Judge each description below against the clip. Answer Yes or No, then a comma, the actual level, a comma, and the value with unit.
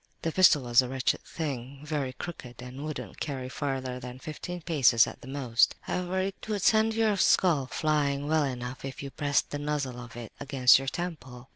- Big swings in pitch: No, average, 3.8 semitones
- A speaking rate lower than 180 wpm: No, average, 190 wpm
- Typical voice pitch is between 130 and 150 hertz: Yes, medium, 140 Hz